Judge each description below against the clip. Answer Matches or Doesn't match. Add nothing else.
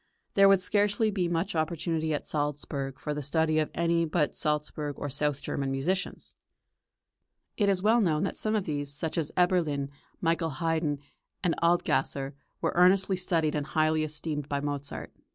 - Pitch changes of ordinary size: Matches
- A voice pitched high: Doesn't match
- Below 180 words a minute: Matches